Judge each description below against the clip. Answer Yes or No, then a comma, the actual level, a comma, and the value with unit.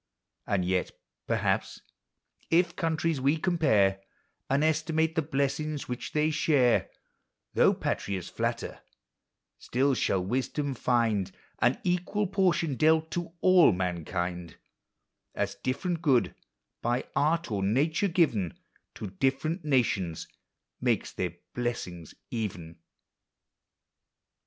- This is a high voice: No, low, 135 Hz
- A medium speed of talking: No, slow, 105 wpm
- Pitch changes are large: Yes, wide, 8.2 semitones